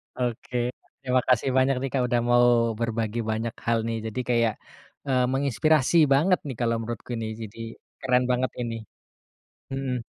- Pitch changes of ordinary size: No, narrow, 2.1 semitones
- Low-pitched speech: Yes, low, 120 Hz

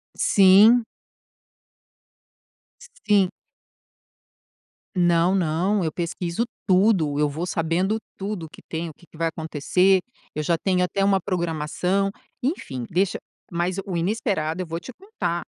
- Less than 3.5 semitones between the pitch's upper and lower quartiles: Yes, average, 3.1 semitones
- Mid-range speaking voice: Yes, medium, 180 Hz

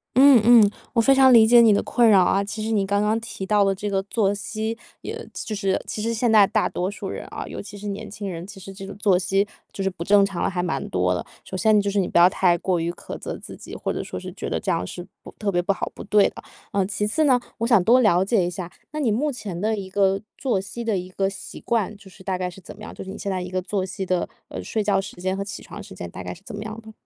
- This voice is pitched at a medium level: No, high, 200 Hz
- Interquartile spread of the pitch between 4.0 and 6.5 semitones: No, narrow, 2.5 semitones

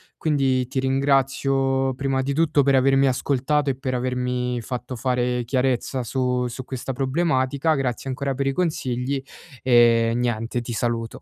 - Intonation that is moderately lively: No, narrow, 1.7 semitones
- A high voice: No, low, 130 Hz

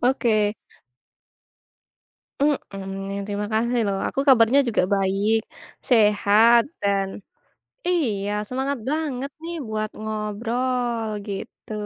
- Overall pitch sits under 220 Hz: No, high, 225 Hz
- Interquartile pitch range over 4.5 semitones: No, average, 3.8 semitones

